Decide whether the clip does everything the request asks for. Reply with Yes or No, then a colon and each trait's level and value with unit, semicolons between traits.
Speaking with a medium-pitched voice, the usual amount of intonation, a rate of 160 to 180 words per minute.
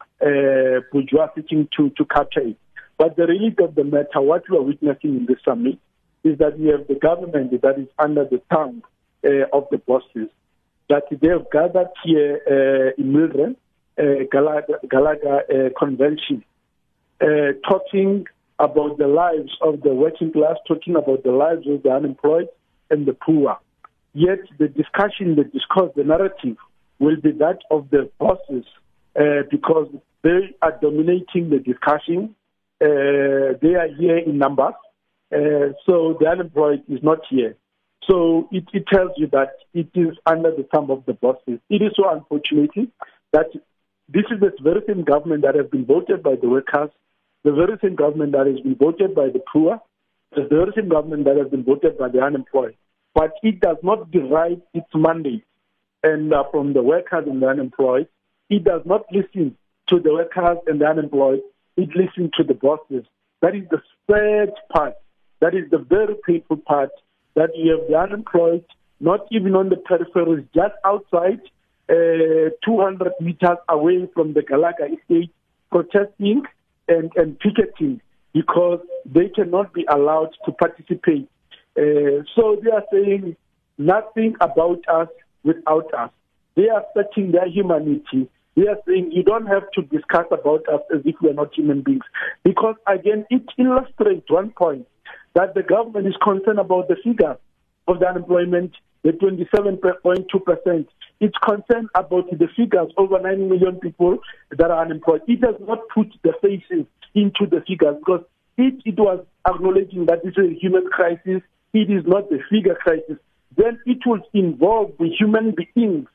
Yes: medium, 170 Hz; average, 4.9 semitones; average, 170 wpm